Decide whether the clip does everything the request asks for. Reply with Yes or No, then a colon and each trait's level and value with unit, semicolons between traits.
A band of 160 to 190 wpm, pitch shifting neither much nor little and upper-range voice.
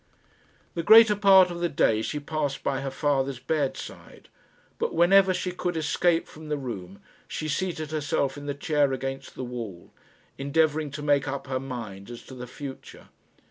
No: average, 175 wpm; average, 3.5 semitones; medium, 145 Hz